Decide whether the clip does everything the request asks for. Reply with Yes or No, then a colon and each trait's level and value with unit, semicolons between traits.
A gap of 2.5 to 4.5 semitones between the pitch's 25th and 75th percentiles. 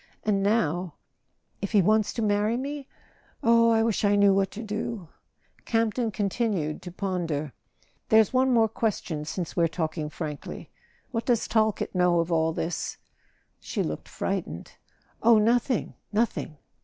No: average, 5.0 semitones